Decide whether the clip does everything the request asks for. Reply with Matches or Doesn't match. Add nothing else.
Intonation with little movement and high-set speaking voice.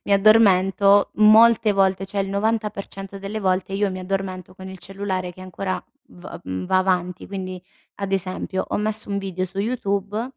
Matches